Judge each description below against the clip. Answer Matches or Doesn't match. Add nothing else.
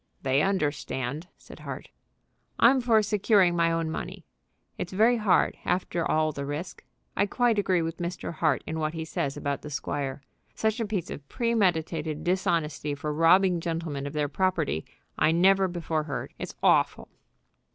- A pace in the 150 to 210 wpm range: Matches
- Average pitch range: Matches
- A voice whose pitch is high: Doesn't match